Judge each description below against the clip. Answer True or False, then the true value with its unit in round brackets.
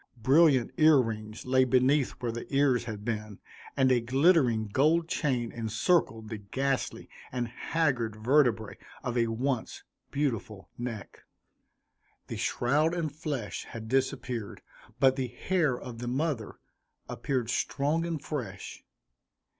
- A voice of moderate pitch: False (125 Hz)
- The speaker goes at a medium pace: False (130 wpm)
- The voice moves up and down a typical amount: True (3.9 semitones)